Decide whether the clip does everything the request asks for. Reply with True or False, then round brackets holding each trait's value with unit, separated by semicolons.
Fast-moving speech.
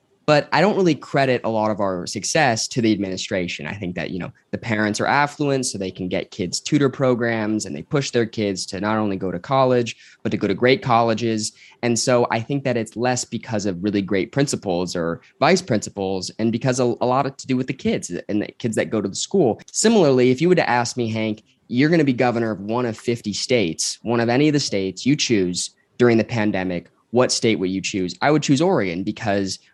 True (240 wpm)